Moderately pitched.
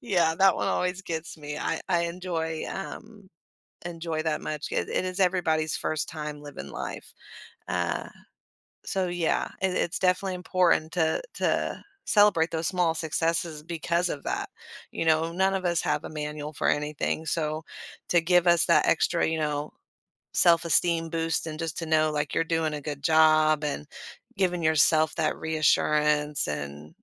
Yes: medium, 160 Hz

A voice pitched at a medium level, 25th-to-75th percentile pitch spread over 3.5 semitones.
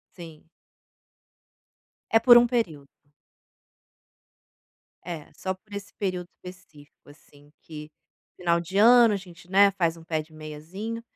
Yes: medium, 180 Hz; average, 4.4 semitones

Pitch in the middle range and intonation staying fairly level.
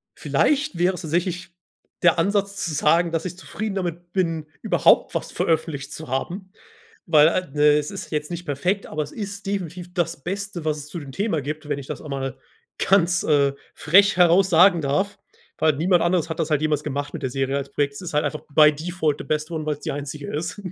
No: medium, 165 Hz; average, 3.5 semitones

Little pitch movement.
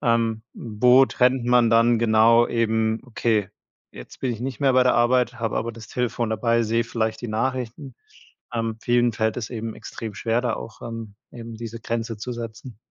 Yes: narrow, 1.5 semitones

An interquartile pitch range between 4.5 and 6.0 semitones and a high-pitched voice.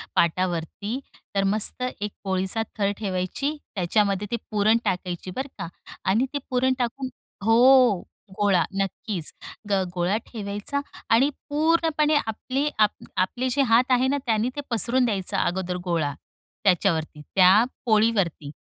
Yes: average, 5.3 semitones; high, 210 Hz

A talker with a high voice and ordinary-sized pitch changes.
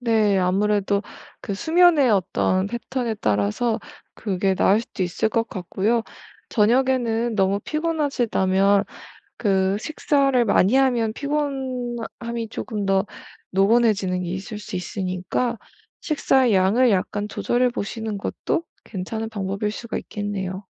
Yes: high, 215 Hz; average, 3.9 semitones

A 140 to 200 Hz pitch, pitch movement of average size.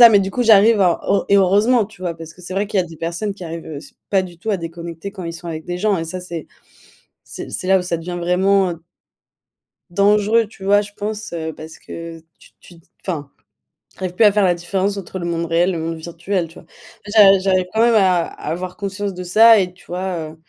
Yes: medium, 185 Hz; average, 3.0 semitones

